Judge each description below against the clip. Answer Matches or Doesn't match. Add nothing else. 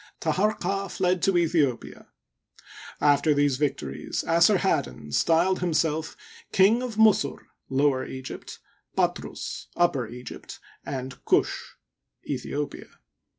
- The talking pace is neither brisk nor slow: Doesn't match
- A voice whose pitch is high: Doesn't match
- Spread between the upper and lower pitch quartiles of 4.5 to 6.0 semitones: Matches